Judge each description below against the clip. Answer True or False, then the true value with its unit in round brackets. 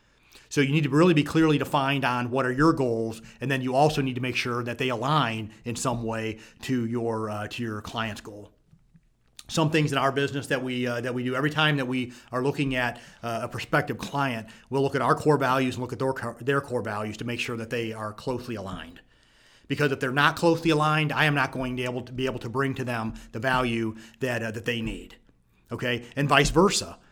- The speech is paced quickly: True (235 wpm)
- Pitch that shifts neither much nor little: True (3.3 semitones)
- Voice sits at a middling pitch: False (125 Hz)